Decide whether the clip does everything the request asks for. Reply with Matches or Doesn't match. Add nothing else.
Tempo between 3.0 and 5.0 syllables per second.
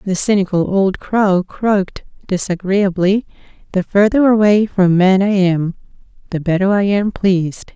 Matches